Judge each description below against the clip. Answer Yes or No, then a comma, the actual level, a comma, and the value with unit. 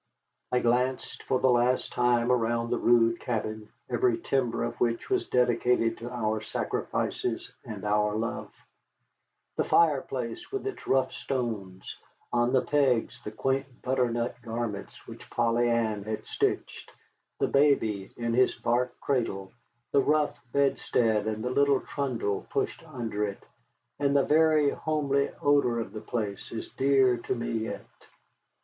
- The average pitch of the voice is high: No, low, 120 Hz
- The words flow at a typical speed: Yes, average, 145 wpm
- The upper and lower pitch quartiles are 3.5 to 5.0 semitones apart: No, average, 2.7 semitones